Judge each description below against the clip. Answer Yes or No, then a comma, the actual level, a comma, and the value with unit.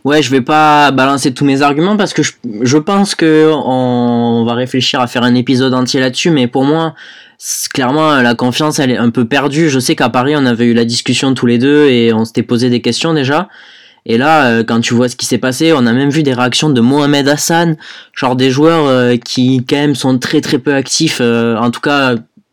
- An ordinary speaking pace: No, fast, 230 wpm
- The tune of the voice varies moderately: Yes, average, 3.5 semitones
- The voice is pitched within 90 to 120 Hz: No, low, 130 Hz